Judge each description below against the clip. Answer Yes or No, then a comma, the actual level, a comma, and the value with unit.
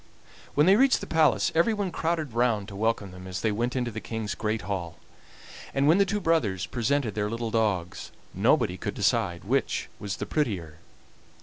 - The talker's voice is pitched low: Yes, low, 110 Hz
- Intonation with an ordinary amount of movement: No, wide, 6.9 semitones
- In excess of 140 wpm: Yes, average, 185 wpm